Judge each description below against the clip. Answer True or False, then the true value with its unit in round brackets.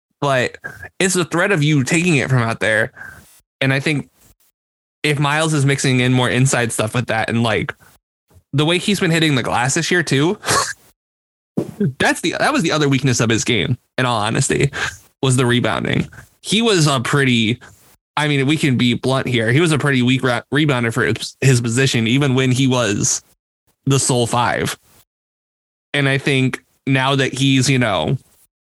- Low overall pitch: True (130 Hz)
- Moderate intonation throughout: True (3.3 semitones)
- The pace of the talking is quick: False (185 wpm)